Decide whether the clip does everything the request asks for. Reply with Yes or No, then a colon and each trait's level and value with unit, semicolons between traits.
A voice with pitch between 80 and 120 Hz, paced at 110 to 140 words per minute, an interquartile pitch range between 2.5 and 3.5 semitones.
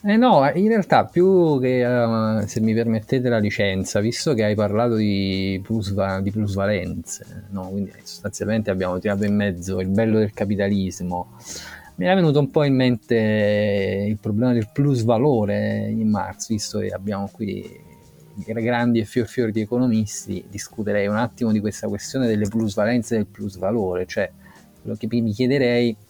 No: low, 110 Hz; average, 165 wpm; average, 2.8 semitones